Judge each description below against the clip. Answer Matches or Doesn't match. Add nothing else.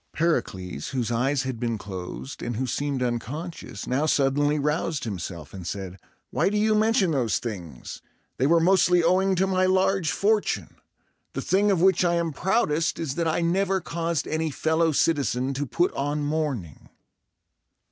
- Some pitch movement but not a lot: Doesn't match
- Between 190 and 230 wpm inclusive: Doesn't match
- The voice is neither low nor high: Matches